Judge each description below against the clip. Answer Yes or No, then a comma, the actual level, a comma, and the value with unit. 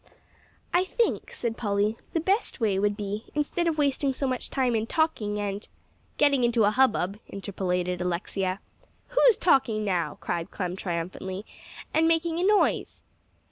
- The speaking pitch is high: Yes, high, 220 Hz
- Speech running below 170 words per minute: Yes, average, 155 wpm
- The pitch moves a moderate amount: No, wide, 7.1 semitones